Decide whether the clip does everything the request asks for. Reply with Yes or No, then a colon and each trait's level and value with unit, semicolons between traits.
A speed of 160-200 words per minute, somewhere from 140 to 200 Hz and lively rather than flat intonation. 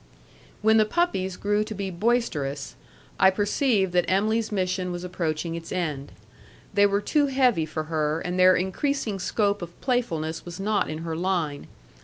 No: average, 165 wpm; medium, 185 Hz; average, 4.2 semitones